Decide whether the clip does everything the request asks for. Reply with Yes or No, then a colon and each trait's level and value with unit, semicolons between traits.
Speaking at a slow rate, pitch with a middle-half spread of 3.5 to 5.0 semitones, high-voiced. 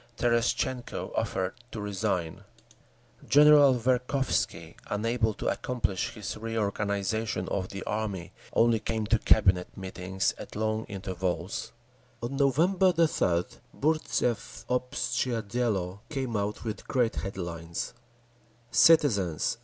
No: slow, 105 wpm; average, 4.5 semitones; low, 110 Hz